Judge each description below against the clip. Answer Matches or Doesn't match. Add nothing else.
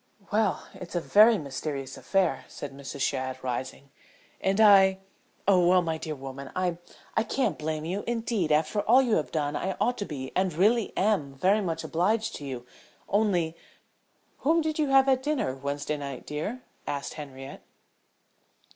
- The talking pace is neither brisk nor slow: Matches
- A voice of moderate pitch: Matches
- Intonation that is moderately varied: Doesn't match